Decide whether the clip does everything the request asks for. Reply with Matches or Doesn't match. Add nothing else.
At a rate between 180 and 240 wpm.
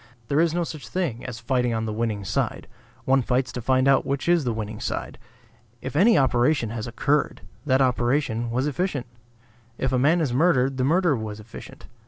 Matches